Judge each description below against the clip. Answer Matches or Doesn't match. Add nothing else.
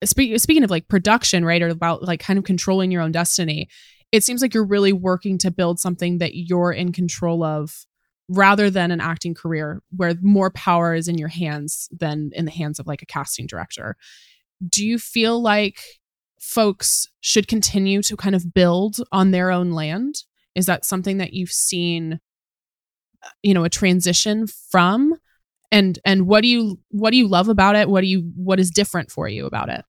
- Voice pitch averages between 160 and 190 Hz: Matches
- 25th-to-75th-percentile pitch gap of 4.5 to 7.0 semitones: Doesn't match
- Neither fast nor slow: Matches